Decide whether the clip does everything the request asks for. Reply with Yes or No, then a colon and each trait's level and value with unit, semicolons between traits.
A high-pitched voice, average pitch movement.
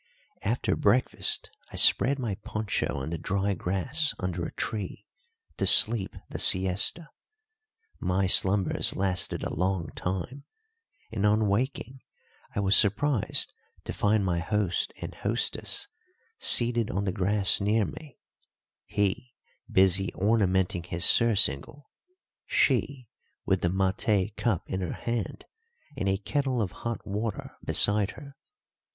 No: low, 100 Hz; average, 3.8 semitones